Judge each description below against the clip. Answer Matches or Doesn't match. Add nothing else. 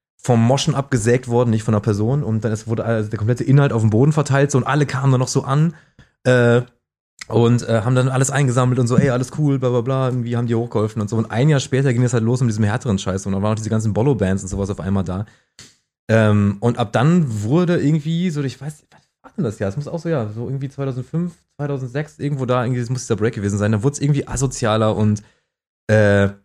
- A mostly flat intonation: Doesn't match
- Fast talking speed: Matches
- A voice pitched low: Matches